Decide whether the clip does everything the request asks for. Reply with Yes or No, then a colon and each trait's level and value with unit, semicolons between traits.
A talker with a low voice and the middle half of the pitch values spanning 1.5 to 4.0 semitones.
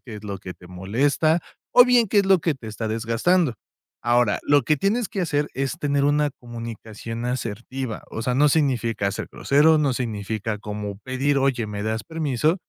No: low, 125 Hz; average, 5.2 semitones